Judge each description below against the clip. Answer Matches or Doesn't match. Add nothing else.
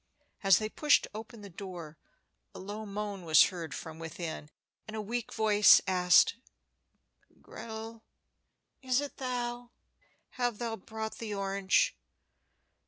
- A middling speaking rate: Doesn't match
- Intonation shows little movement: Doesn't match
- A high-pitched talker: Matches